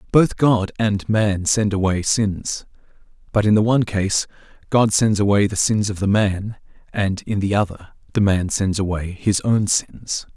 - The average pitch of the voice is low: Yes, low, 100 Hz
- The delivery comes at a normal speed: Yes, average, 180 wpm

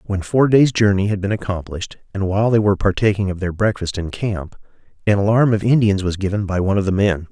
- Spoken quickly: Yes, fast, 230 wpm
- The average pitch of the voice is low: Yes, low, 100 Hz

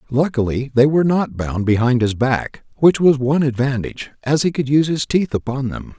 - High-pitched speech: No, low, 130 Hz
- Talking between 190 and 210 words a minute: Yes, average, 200 wpm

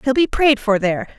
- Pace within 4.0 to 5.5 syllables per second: No, 6.0 syllables/s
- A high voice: Yes, high, 245 Hz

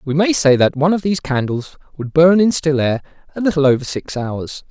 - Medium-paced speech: No, fast, 230 wpm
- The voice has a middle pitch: Yes, medium, 150 Hz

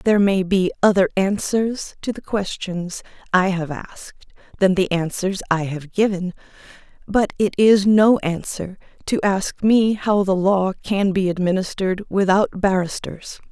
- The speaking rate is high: No, average, 145 wpm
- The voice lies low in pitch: No, high, 190 Hz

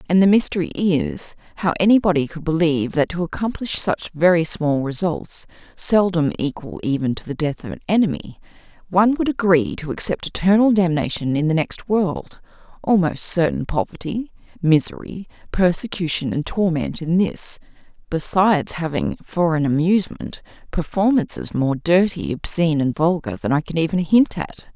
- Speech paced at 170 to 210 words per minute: No, average, 150 wpm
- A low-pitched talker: No, medium, 170 Hz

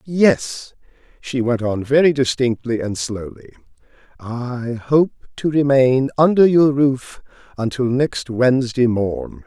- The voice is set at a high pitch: No, low, 130 Hz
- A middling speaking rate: No, slow, 120 wpm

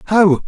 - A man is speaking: Yes, male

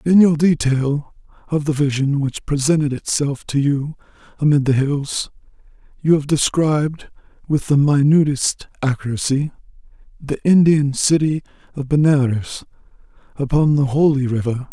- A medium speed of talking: No, slow, 120 wpm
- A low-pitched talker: No, medium, 145 Hz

